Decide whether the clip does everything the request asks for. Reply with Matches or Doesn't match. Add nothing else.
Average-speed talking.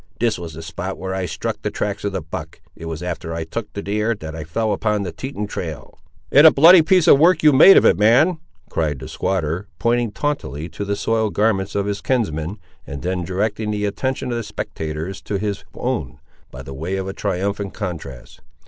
Doesn't match